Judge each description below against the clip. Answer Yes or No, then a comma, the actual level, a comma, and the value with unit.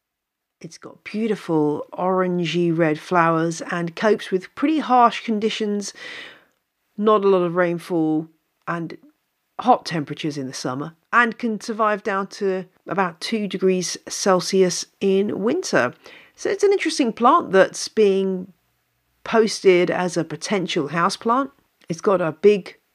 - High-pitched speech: Yes, high, 195 Hz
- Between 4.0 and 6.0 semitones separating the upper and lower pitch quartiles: Yes, average, 4.4 semitones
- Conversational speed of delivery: No, slow, 130 wpm